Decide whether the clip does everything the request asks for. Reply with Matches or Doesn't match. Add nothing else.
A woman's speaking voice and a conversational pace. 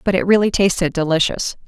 Matches